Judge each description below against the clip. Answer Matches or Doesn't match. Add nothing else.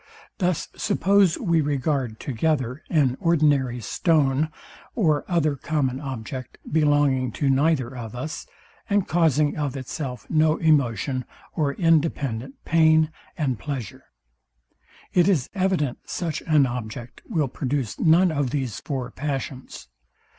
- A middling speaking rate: Doesn't match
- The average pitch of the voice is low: Doesn't match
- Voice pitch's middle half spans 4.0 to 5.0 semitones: Doesn't match